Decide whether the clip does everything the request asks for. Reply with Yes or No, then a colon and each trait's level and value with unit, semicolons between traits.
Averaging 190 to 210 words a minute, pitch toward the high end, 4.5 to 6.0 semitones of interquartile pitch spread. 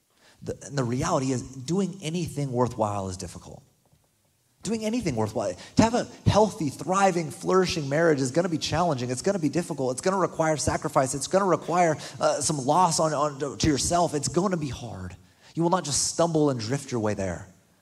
No: average, 200 wpm; medium, 150 Hz; average, 5.3 semitones